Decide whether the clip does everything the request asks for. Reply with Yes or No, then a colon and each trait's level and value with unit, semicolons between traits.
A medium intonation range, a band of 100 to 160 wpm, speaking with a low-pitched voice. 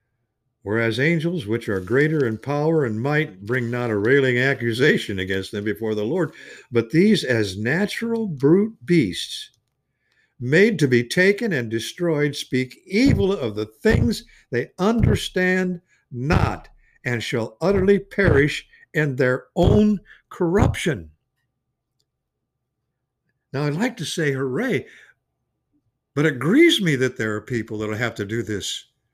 No: wide, 6.1 semitones; slow, 135 wpm; low, 130 Hz